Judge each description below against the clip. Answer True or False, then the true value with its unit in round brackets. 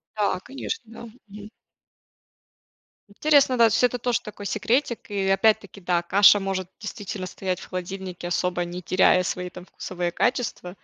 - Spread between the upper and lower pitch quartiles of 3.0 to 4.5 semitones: True (3.4 semitones)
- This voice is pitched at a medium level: False (195 Hz)